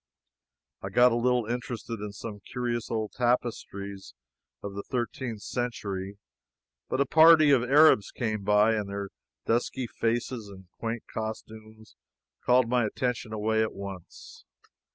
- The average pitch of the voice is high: No, low, 115 Hz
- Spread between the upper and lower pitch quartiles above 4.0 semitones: No, average, 2.9 semitones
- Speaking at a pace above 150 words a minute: No, slow, 135 wpm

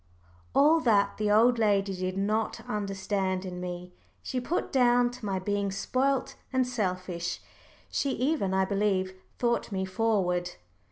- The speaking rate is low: No, average, 145 wpm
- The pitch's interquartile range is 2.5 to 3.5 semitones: No, average, 4.3 semitones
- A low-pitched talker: No, high, 205 Hz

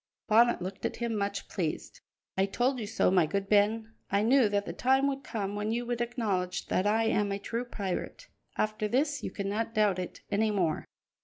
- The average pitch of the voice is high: Yes, high, 215 Hz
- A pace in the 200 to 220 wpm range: Yes, fast, 205 wpm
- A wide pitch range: No, average, 3.0 semitones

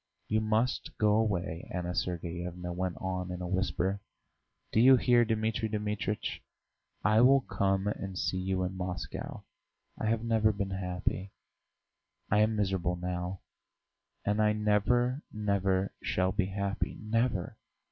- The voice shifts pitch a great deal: No, average, 2.9 semitones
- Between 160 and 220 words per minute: No, slow, 135 wpm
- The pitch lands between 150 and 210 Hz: No, low, 100 Hz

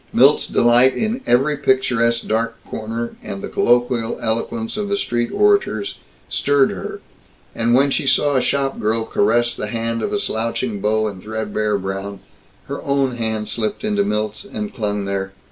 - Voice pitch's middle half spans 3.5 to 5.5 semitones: Yes, average, 4.1 semitones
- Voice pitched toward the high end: No, low, 115 Hz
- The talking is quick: No, average, 160 wpm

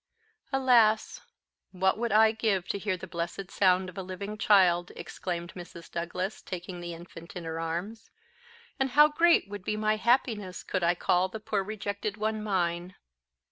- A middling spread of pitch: Yes, average, 3.4 semitones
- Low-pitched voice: No, high, 195 Hz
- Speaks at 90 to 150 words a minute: No, average, 170 wpm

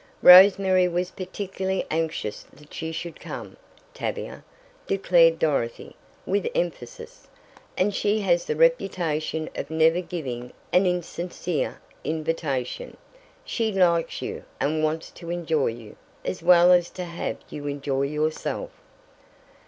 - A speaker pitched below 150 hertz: No, medium, 170 Hz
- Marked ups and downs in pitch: No, average, 3.0 semitones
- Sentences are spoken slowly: Yes, slow, 125 wpm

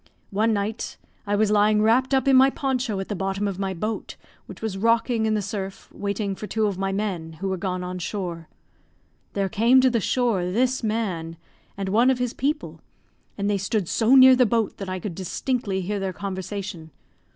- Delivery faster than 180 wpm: Yes, fast, 205 wpm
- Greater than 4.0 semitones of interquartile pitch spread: No, average, 3.2 semitones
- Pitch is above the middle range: Yes, high, 205 Hz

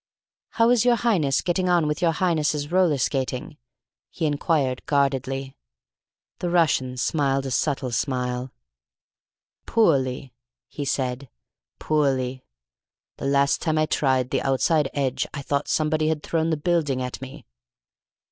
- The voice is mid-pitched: Yes, medium, 145 Hz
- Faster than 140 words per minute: No, slow, 135 wpm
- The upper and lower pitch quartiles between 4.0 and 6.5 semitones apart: No, average, 3.3 semitones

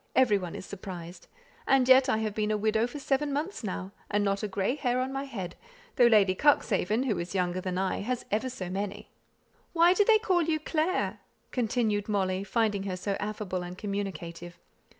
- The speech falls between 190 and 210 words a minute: Yes, average, 195 wpm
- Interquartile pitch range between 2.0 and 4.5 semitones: No, average, 5.3 semitones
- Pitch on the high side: Yes, high, 210 Hz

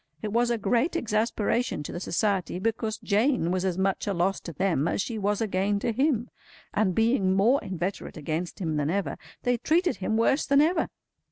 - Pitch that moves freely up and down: No, average, 4.1 semitones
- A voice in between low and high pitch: No, high, 205 Hz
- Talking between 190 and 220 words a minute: Yes, average, 200 wpm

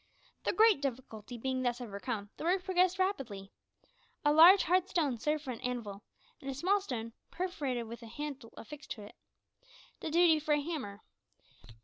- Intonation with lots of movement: Yes, wide, 6.7 semitones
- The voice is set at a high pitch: Yes, very high, 275 Hz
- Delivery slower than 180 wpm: Yes, average, 170 wpm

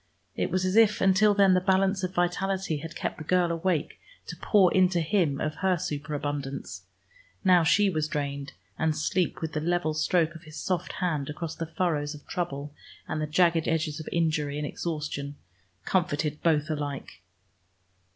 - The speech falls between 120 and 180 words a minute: Yes, average, 170 wpm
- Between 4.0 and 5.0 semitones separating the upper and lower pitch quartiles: No, average, 3.5 semitones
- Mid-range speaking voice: Yes, medium, 165 Hz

